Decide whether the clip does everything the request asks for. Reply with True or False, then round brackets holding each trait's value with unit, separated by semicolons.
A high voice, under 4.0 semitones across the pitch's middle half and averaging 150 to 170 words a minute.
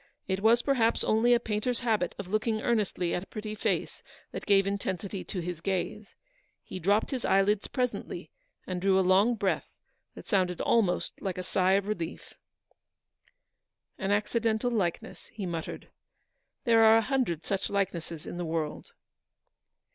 True (200 Hz; 3.4 semitones; 155 wpm)